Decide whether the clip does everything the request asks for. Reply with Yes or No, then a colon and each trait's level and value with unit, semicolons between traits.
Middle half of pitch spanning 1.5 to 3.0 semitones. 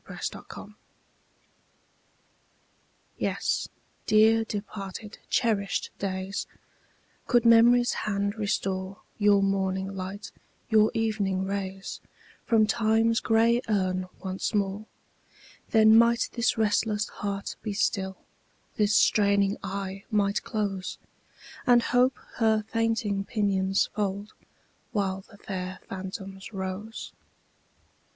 Yes: narrow, 2.4 semitones